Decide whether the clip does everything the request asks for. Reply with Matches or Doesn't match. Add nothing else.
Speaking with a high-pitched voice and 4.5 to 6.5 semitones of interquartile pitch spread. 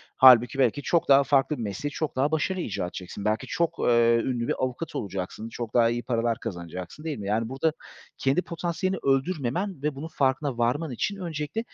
Doesn't match